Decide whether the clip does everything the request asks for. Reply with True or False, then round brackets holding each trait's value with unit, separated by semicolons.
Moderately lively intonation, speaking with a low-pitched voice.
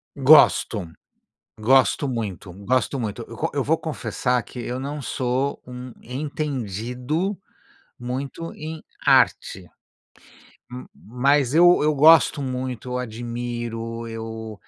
True (3.4 semitones; 125 Hz)